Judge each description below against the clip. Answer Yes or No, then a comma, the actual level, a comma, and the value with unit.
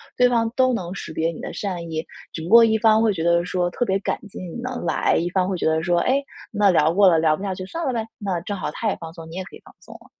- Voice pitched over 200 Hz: No, medium, 185 Hz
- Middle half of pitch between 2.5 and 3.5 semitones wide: No, average, 4.5 semitones